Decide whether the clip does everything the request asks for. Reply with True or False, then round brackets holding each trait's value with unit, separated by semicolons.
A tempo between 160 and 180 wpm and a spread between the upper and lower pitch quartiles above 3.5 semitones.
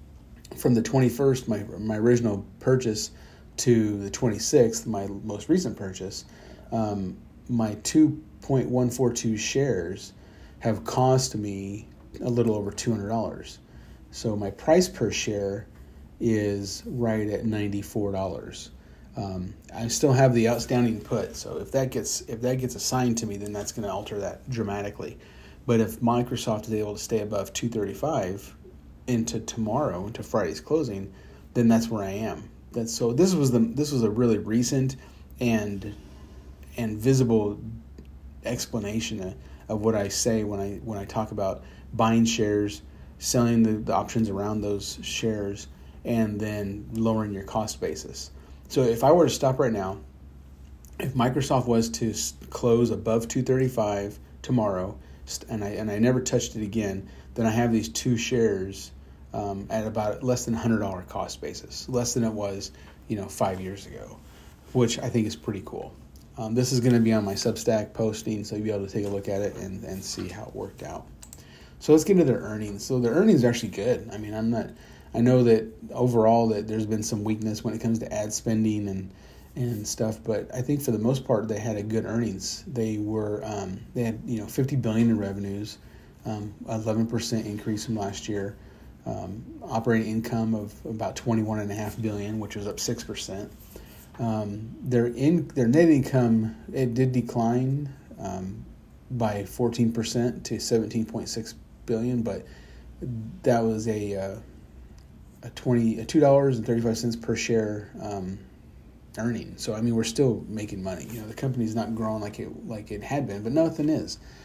False (175 wpm; 2.7 semitones)